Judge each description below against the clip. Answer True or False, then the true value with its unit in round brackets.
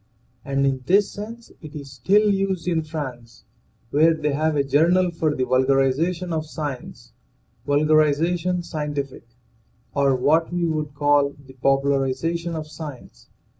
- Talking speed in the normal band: True (145 wpm)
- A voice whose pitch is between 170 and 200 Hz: False (150 Hz)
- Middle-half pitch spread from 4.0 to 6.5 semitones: False (3.5 semitones)